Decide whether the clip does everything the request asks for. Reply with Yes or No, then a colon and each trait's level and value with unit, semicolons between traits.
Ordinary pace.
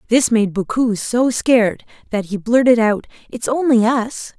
Yes: average, 165 wpm